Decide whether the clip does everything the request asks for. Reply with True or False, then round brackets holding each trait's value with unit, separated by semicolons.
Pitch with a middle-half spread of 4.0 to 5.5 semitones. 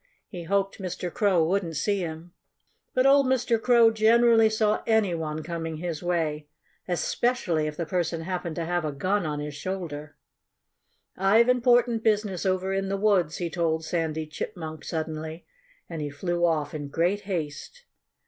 True (4.5 semitones)